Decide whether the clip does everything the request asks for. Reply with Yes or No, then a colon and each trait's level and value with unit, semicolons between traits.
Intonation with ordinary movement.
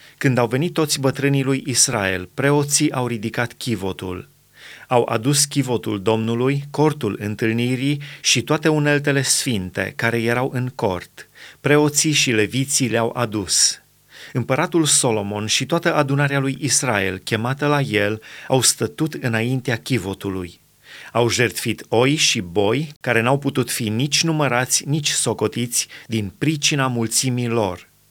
Yes: average, 4.0 semitones